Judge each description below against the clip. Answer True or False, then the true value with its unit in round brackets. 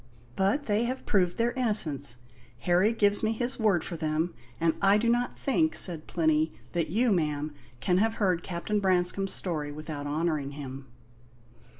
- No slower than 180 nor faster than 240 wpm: False (165 wpm)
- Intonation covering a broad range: True (5.7 semitones)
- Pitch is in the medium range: True (180 Hz)